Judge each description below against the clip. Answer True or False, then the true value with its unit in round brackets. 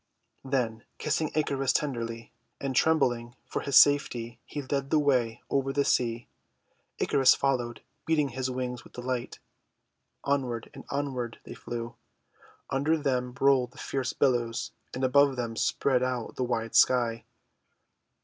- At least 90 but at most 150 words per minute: True (140 wpm)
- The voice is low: True (130 Hz)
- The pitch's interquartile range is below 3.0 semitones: True (2.6 semitones)